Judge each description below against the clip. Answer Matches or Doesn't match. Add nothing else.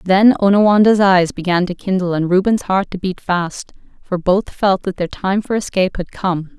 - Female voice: Matches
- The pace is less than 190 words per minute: Doesn't match